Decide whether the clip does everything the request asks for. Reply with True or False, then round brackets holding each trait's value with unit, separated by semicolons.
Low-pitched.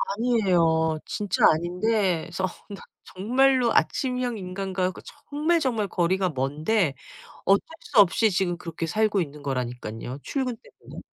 False (190 Hz)